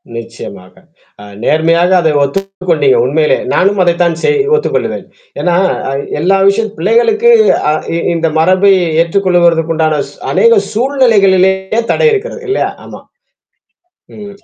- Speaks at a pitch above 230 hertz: No, high, 190 Hz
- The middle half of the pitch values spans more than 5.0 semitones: Yes, wide, 5.4 semitones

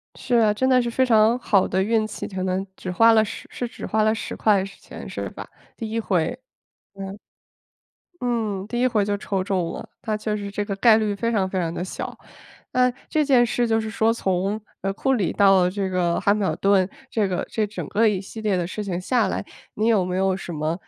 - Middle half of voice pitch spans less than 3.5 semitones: Yes, average, 3.0 semitones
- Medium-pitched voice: No, high, 205 Hz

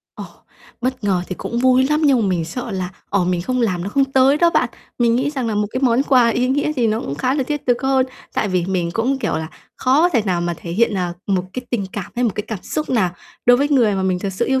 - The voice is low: No, high, 235 Hz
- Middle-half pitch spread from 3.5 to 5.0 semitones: No, wide, 5.6 semitones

